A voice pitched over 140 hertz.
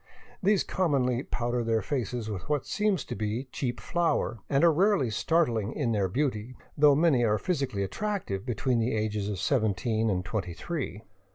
No: low, 120 Hz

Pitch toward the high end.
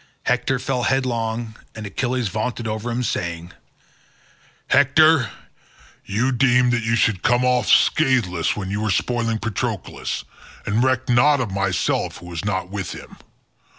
No: low, 115 Hz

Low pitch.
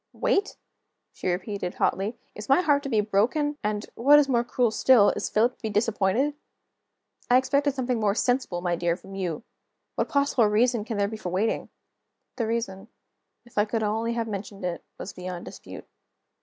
No: high, 220 Hz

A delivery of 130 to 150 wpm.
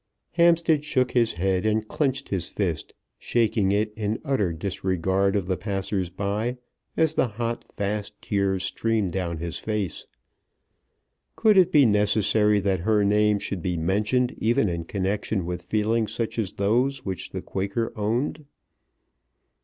Yes: average, 145 wpm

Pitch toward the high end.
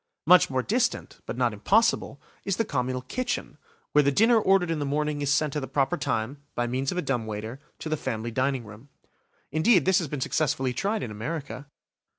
No: medium, 140 Hz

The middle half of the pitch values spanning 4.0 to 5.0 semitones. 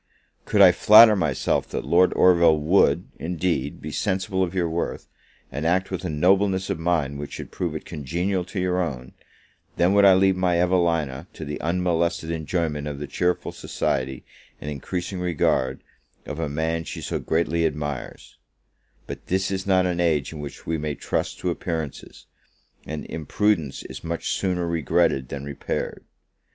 No: average, 3.6 semitones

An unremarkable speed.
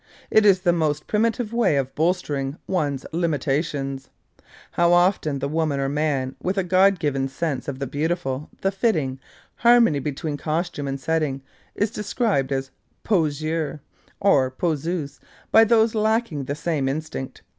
Yes: average, 150 wpm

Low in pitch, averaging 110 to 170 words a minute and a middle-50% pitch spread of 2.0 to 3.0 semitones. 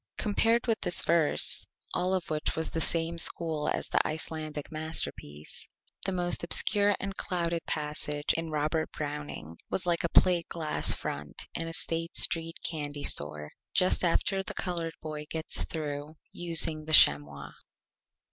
No: medium, 160 Hz; average, 155 wpm; narrow, 2.4 semitones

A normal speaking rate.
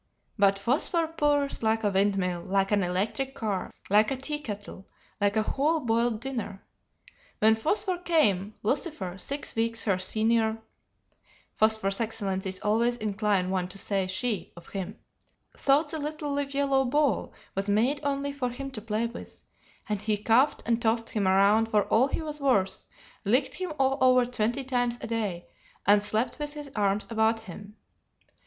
Yes: average, 165 wpm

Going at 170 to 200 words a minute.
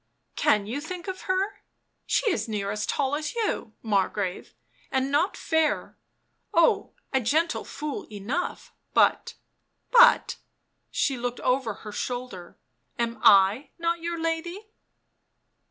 No: average, 155 wpm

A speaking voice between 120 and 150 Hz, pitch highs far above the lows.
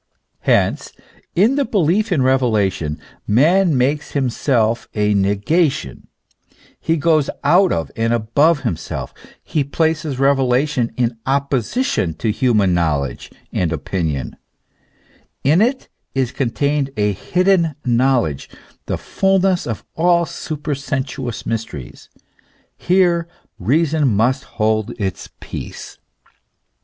Yes: low, 135 Hz; wide, 6.9 semitones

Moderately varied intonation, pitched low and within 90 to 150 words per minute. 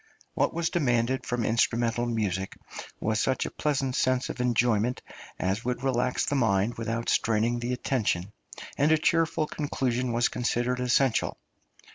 No: narrow, 2.2 semitones; low, 120 Hz; average, 145 wpm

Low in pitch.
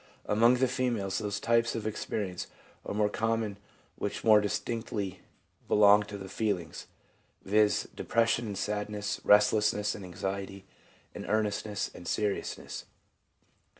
Yes: low, 105 Hz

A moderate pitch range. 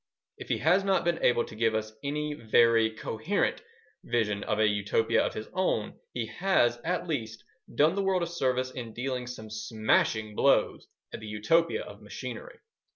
No: wide, 7.0 semitones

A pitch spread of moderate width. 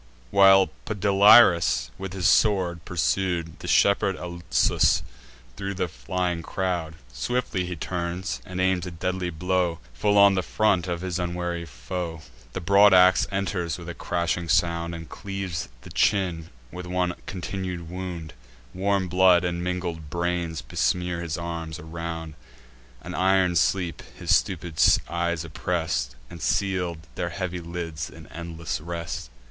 No: narrow, 1.8 semitones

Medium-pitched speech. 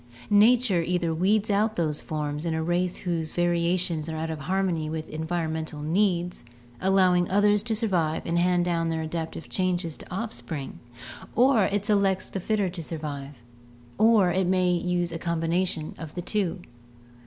Yes: medium, 175 Hz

